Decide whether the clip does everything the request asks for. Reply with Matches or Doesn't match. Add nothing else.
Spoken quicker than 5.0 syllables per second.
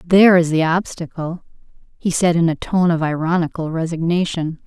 Matches